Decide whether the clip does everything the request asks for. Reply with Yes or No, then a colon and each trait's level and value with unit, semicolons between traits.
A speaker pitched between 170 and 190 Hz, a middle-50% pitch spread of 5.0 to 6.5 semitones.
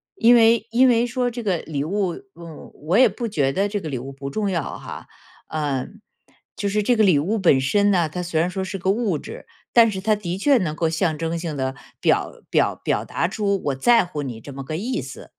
Yes: medium, 185 Hz; wide, 5.6 semitones